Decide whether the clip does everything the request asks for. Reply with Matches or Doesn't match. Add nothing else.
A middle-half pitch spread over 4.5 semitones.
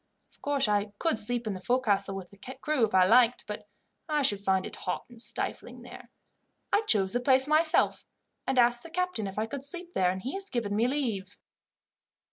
Matches